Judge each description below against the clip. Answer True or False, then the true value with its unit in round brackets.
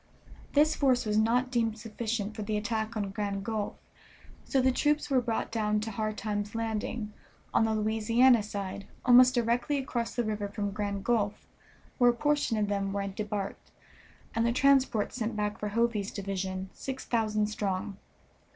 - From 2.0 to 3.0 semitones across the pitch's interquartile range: True (2.5 semitones)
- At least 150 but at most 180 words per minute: True (170 wpm)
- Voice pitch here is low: False (220 Hz)